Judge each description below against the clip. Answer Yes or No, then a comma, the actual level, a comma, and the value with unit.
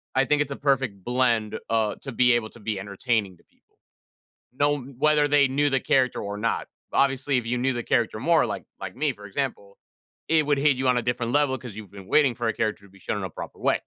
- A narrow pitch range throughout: No, average, 4.1 semitones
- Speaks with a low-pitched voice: Yes, low, 125 Hz